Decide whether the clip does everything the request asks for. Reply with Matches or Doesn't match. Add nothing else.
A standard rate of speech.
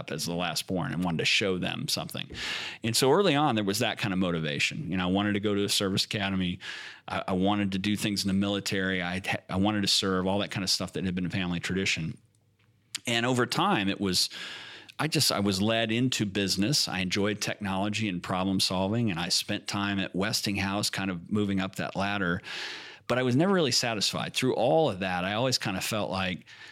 Doesn't match